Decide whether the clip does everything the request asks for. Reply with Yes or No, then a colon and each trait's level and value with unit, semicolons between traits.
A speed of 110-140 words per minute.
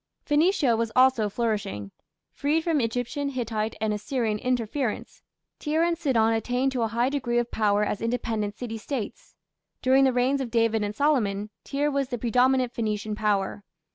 No: average, 165 wpm